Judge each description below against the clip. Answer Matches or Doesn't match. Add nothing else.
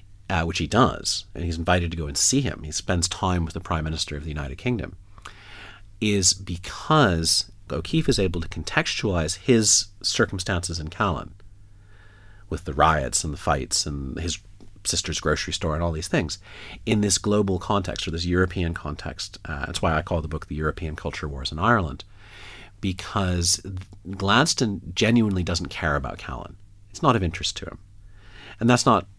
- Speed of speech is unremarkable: Matches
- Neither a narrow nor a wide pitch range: Matches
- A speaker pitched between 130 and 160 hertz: Doesn't match